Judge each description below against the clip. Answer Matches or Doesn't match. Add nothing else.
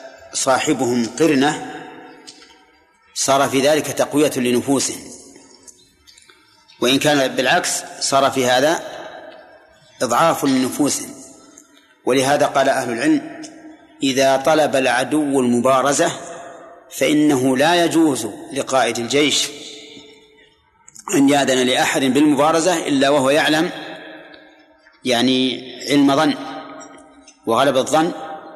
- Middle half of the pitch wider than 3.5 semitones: Matches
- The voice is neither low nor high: Matches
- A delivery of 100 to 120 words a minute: Doesn't match